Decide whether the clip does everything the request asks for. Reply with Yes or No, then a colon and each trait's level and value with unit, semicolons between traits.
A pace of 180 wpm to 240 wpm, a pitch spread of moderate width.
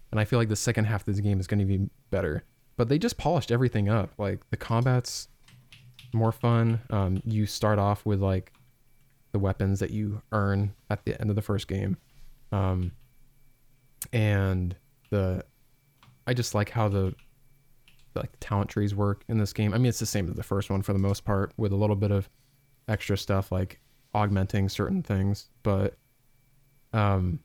Yes: average, 190 wpm; average, 4.1 semitones